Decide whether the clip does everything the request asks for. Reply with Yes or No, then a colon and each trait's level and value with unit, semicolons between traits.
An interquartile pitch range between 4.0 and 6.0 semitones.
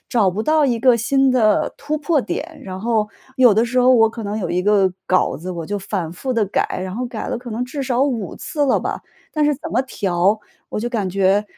Yes: average, 4.7 semitones